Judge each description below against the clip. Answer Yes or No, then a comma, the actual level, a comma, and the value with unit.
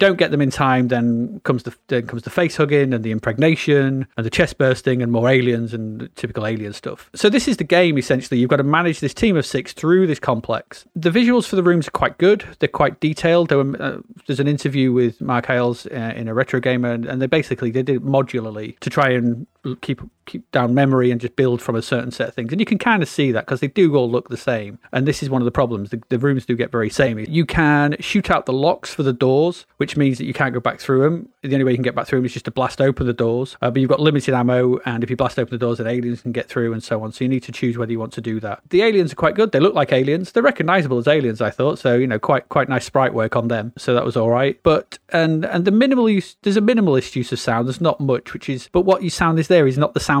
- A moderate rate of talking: No, fast, 290 wpm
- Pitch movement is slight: No, average, 4.3 semitones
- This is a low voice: Yes, low, 130 Hz